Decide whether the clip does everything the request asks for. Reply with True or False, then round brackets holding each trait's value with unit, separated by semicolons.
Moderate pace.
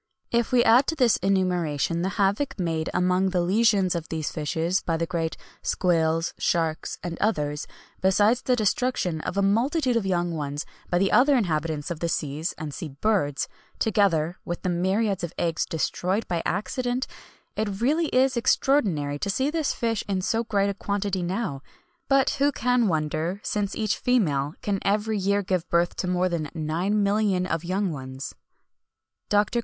True (170 wpm)